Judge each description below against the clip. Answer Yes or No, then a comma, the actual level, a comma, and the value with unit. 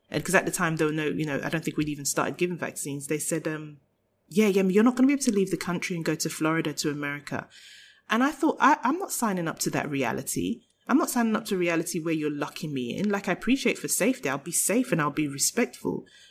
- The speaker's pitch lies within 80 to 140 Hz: No, medium, 170 Hz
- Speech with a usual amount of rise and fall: No, wide, 6.2 semitones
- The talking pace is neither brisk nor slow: No, fast, 270 wpm